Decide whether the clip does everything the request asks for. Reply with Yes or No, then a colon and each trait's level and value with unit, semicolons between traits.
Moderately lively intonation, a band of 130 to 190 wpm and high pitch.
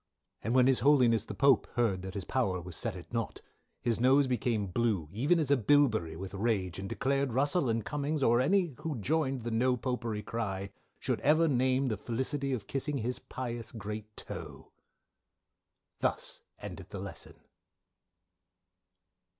No: average, 4.3 semitones; average, 165 wpm; low, 120 Hz